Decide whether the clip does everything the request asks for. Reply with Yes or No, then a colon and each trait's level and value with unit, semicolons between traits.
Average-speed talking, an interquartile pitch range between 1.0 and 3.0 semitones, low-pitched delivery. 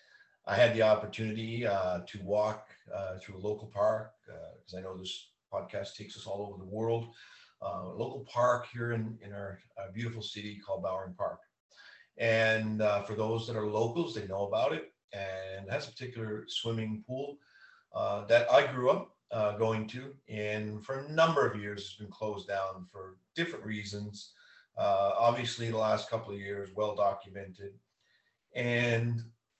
Yes: average, 175 wpm; narrow, 2.6 semitones; low, 110 Hz